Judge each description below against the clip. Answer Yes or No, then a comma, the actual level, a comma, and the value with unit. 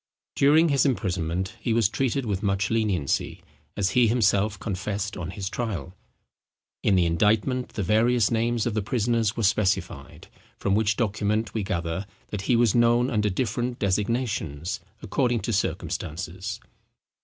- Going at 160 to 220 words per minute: No, average, 145 wpm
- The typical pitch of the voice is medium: No, low, 105 Hz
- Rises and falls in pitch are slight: No, average, 3.6 semitones